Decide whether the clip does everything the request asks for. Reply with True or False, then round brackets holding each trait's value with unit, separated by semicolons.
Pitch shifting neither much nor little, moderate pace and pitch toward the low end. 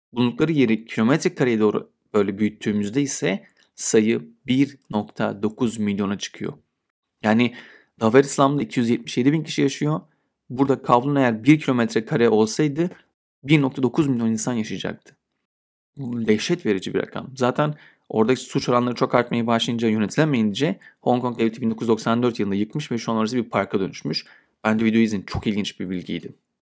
False (4.0 semitones; 145 wpm; 120 Hz)